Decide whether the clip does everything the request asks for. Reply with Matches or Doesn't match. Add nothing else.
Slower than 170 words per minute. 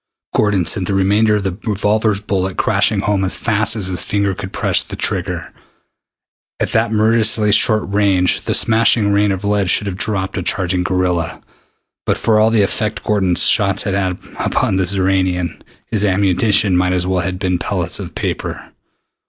Doesn't match